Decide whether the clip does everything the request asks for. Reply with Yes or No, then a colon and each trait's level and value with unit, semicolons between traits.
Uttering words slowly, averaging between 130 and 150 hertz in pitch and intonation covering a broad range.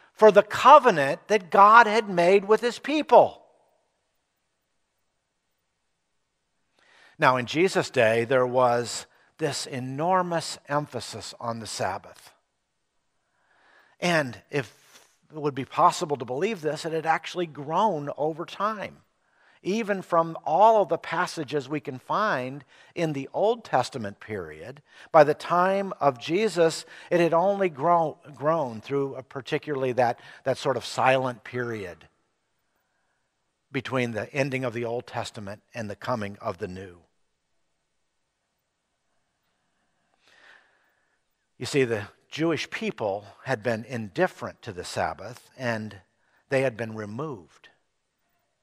Yes: slow, 120 wpm; medium, 140 Hz; wide, 6.4 semitones